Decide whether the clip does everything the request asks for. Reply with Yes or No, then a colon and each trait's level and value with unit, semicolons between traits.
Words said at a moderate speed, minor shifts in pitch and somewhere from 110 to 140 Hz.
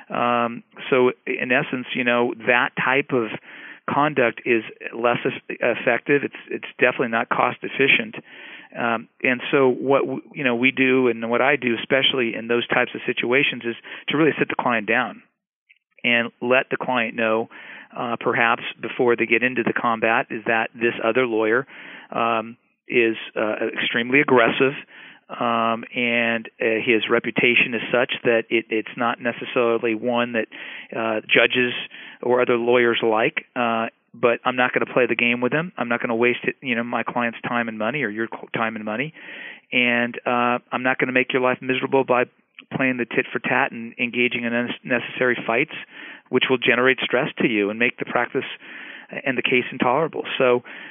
Yes: average, 180 wpm; narrow, 1.7 semitones; low, 120 Hz